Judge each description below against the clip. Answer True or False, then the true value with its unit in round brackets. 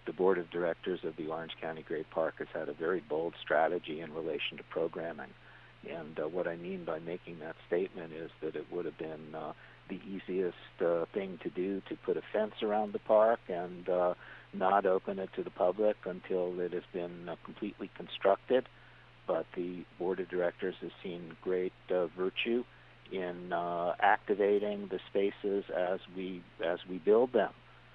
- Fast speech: False (185 wpm)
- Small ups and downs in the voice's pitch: True (2.3 semitones)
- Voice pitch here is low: True (90 Hz)